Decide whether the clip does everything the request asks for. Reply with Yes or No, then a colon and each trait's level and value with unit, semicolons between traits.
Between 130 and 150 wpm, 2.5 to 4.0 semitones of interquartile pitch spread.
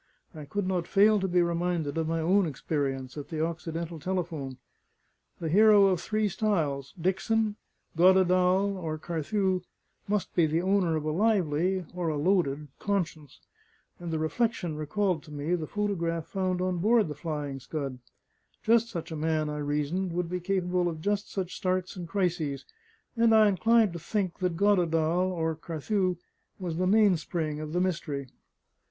No: average, 165 wpm; average, 3.5 semitones